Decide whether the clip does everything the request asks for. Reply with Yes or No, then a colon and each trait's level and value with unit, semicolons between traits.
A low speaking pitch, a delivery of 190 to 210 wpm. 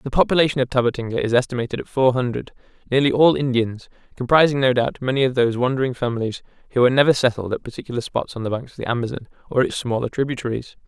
Yes: low, 125 Hz; fast, 205 wpm